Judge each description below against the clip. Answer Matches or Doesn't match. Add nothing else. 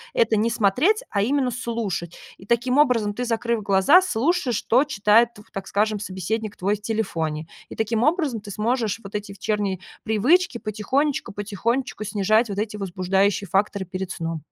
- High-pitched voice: Matches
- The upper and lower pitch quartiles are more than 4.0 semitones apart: Doesn't match